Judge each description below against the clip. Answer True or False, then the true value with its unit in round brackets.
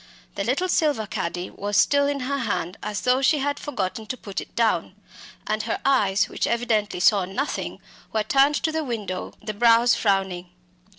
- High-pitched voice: True (220 Hz)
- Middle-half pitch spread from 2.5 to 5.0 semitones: False (5.5 semitones)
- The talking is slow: False (180 wpm)